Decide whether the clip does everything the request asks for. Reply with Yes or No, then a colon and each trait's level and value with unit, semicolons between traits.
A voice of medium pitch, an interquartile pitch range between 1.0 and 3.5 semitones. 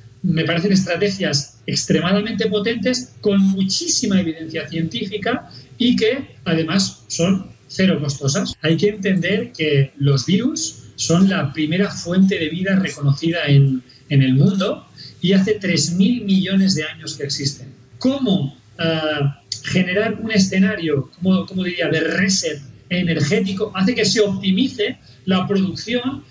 No: medium, 180 Hz; average, 5.3 semitones